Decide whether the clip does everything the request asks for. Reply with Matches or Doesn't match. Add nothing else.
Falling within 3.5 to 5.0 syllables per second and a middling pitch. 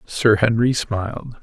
Doesn't match